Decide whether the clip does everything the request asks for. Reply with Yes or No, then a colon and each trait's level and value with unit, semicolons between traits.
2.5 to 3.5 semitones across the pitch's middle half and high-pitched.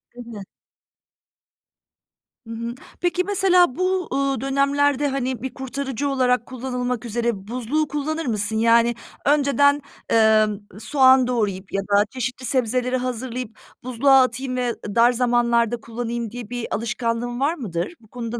Yes: average, 2.9 semitones; high, 245 Hz